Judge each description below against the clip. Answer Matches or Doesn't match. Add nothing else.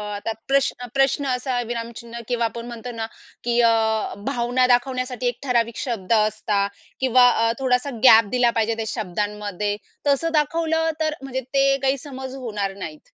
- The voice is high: Matches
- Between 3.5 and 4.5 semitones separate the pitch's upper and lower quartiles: Doesn't match